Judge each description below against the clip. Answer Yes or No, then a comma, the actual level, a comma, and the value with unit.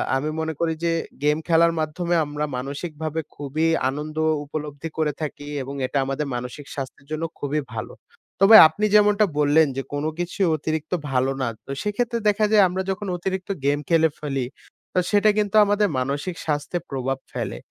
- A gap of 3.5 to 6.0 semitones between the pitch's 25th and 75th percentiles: Yes, average, 3.8 semitones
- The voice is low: No, medium, 155 Hz